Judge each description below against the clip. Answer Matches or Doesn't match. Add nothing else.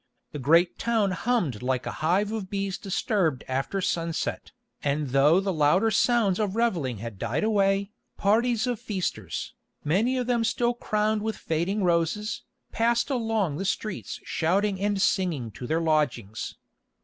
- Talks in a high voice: Matches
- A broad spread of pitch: Matches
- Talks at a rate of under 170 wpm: Matches